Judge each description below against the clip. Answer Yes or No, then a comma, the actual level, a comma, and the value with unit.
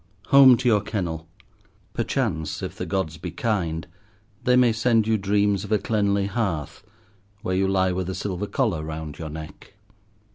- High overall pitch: No, very low, 95 Hz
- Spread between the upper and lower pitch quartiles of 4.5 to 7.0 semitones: Yes, average, 5.0 semitones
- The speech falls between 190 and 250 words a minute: No, average, 170 wpm